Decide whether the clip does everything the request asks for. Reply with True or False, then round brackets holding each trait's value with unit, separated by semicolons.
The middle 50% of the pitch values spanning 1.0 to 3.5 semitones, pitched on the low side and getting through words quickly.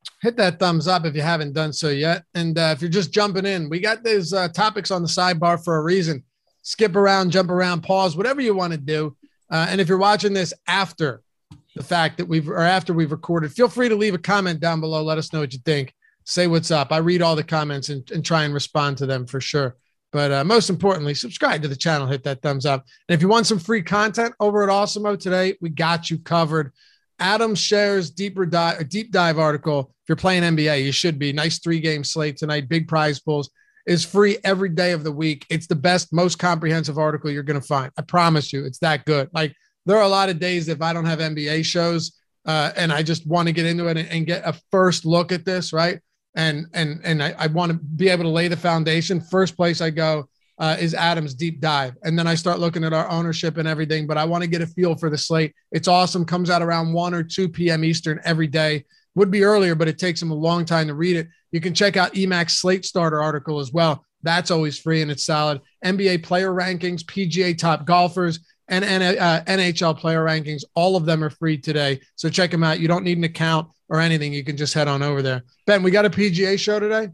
False (2.7 semitones; 165 Hz; 245 wpm)